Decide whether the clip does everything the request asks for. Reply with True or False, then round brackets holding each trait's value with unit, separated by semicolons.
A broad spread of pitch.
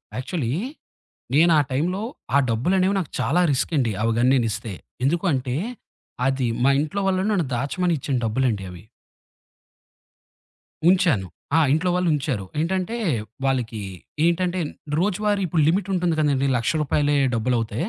True (6.3 semitones)